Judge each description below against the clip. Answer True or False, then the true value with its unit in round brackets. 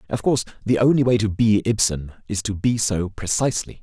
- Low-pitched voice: True (110 Hz)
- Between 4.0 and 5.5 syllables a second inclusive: False (5.8 syllables/s)